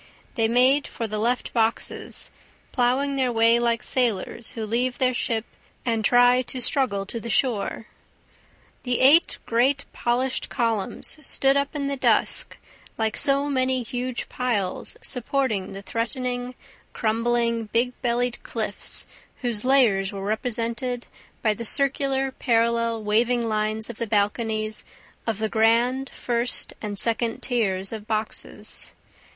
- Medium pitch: No, high, 235 Hz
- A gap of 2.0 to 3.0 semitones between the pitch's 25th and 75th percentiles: Yes, narrow, 2.5 semitones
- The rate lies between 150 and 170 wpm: No, slow, 135 wpm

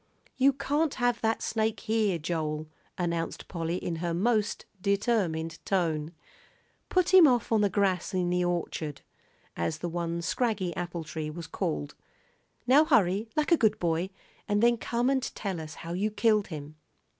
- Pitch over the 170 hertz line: Yes, medium, 185 Hz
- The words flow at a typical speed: Yes, average, 165 wpm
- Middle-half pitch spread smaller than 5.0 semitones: No, average, 5.3 semitones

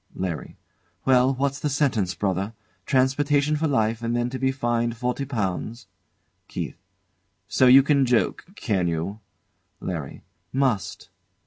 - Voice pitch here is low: Yes, low, 125 Hz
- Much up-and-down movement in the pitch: No, average, 4.7 semitones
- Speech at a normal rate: No, slow, 130 wpm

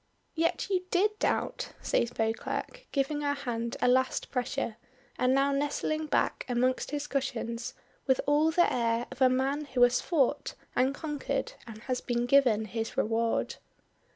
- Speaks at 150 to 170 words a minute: Yes, average, 155 wpm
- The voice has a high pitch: Yes, very high, 260 Hz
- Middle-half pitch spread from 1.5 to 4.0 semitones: Yes, average, 3.4 semitones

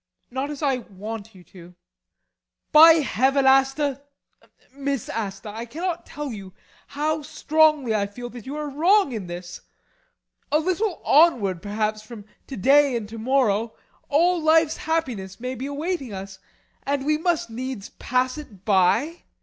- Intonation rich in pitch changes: Yes, wide, 6.0 semitones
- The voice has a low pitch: No, very high, 265 Hz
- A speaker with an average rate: Yes, average, 160 wpm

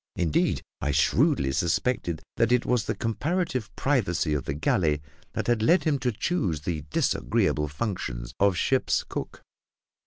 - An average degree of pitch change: No, wide, 8.8 semitones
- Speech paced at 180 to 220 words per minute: No, average, 150 wpm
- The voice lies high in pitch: No, very low, 95 Hz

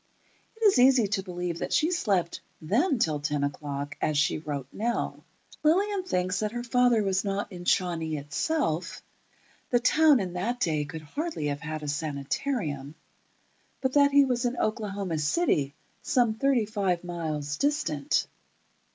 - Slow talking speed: No, average, 155 wpm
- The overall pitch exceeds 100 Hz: Yes, high, 190 Hz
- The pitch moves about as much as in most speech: No, wide, 8.3 semitones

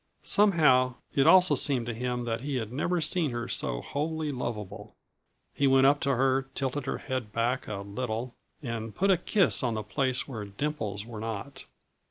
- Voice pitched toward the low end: Yes, low, 130 Hz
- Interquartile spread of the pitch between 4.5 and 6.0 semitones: No, average, 4.1 semitones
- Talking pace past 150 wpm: Yes, average, 185 wpm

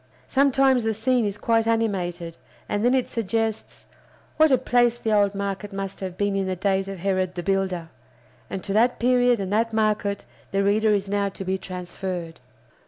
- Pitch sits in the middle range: No, high, 200 Hz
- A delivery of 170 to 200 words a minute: Yes, average, 185 wpm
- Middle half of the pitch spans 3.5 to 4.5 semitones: No, average, 3.1 semitones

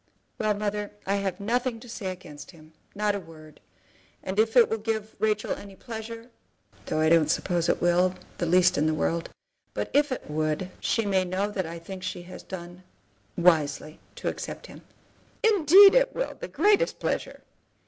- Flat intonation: No, average, 4.7 semitones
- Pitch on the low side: No, high, 190 Hz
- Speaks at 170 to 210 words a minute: Yes, average, 180 wpm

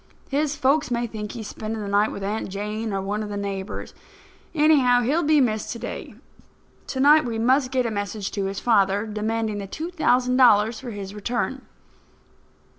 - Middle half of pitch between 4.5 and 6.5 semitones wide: No, average, 4.1 semitones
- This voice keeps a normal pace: Yes, average, 190 wpm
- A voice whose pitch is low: No, high, 225 Hz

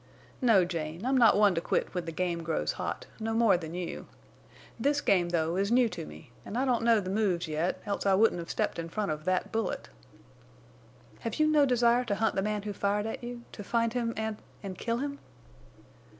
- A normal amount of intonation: Yes, average, 4.8 semitones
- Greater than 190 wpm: Yes, fast, 205 wpm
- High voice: Yes, high, 205 Hz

